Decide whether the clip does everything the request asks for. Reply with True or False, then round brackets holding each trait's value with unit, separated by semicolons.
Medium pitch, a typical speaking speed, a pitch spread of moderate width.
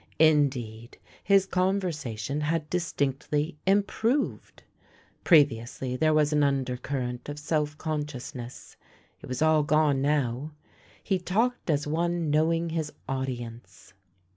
False (150 Hz; 120 wpm; 3.7 semitones)